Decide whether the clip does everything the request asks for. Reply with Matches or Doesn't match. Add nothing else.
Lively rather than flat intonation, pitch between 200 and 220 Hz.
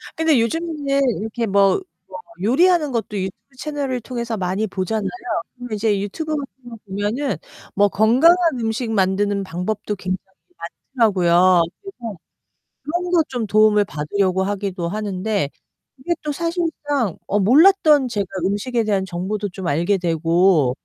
Matches